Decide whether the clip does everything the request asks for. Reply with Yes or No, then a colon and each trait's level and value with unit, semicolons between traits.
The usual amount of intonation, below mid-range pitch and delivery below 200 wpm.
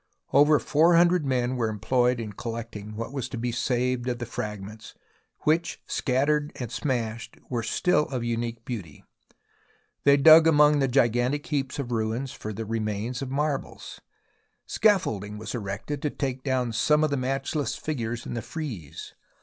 Yes: average, 4.1 semitones; low, 125 Hz; average, 160 wpm